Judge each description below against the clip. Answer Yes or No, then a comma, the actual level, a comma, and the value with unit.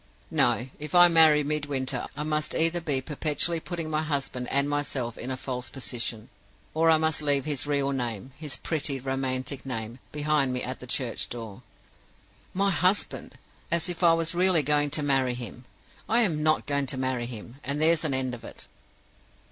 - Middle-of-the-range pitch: Yes, medium, 145 Hz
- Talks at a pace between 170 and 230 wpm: Yes, average, 185 wpm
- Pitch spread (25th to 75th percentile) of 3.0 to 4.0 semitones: Yes, average, 3.4 semitones